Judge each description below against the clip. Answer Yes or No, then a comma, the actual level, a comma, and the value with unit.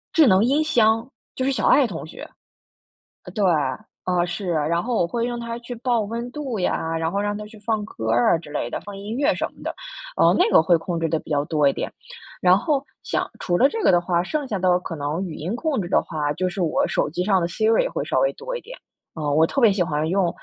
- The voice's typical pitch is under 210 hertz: Yes, high, 195 Hz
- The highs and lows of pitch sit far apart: Yes, wide, 6.2 semitones